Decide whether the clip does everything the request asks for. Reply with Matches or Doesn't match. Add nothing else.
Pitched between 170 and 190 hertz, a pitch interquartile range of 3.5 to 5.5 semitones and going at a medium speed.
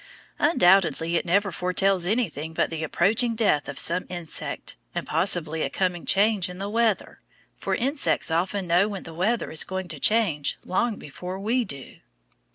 Matches